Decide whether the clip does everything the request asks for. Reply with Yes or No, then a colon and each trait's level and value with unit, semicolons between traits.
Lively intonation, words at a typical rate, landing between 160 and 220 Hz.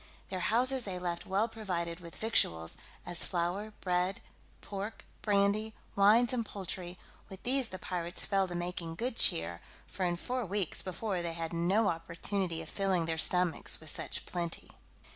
No: average, 3.4 semitones; average, 160 wpm; medium, 185 Hz